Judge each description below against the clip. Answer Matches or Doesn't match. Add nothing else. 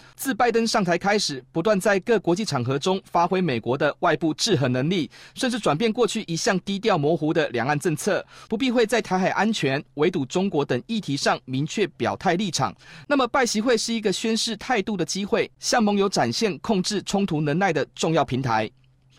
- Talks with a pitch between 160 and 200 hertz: Matches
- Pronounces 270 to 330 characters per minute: Matches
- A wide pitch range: Matches